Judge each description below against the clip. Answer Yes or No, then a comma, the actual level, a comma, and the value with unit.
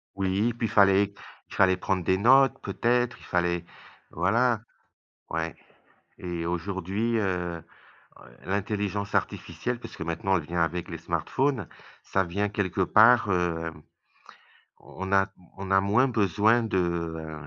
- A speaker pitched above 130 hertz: No, very low, 95 Hz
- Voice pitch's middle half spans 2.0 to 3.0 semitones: No, average, 3.6 semitones